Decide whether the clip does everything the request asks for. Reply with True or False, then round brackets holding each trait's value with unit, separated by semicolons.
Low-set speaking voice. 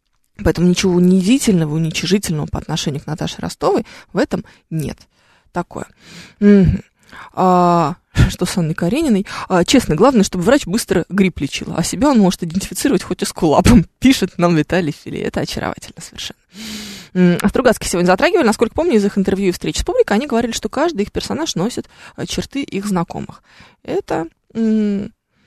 False (190 Hz)